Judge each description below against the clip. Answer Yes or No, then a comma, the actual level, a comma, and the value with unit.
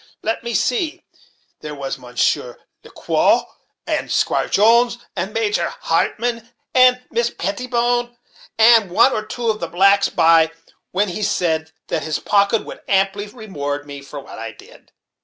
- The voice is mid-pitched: No, high, 205 Hz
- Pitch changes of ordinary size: No, wide, 6.4 semitones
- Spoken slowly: No, average, 155 wpm